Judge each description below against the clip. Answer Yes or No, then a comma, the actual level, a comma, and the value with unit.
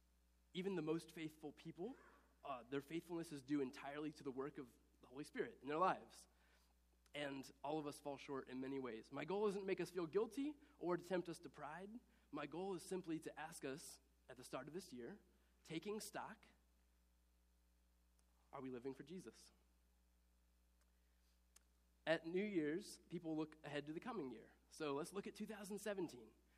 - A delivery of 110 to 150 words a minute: No, average, 180 wpm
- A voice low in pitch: No, medium, 145 Hz